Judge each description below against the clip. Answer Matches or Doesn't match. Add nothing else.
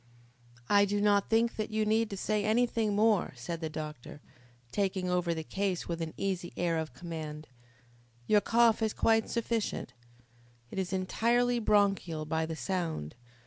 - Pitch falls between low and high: Doesn't match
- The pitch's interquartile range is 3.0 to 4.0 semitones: Doesn't match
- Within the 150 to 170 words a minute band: Matches